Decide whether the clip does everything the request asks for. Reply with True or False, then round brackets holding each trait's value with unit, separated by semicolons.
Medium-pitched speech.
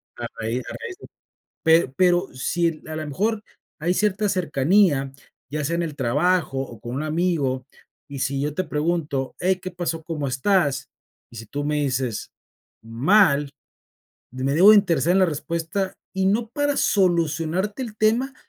True (165 Hz)